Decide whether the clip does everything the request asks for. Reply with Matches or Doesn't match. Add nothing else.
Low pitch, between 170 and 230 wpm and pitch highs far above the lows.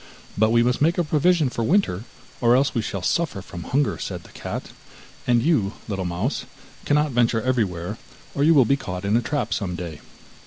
Matches